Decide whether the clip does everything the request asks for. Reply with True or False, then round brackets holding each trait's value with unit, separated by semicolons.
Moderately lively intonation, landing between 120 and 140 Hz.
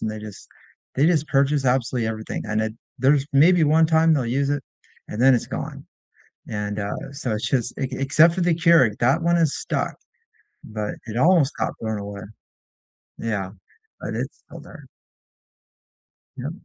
False (6.2 semitones; 135 Hz)